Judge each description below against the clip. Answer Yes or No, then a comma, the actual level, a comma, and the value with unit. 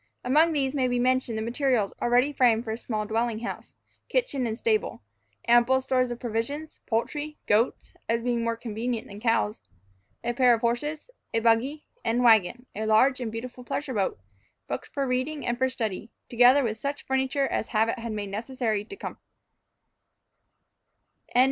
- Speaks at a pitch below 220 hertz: No, high, 240 Hz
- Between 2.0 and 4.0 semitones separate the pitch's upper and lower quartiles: Yes, average, 2.7 semitones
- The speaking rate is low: No, average, 165 wpm